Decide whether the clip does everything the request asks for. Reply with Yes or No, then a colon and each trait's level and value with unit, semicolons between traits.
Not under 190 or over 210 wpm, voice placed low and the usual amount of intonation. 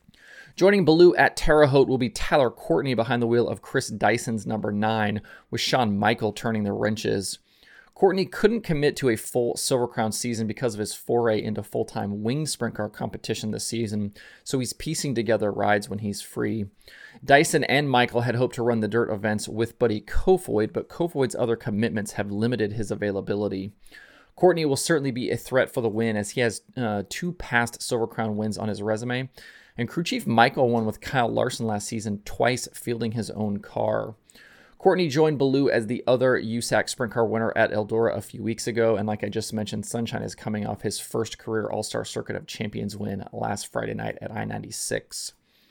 Yes: average, 195 wpm; low, 115 Hz; average, 3.0 semitones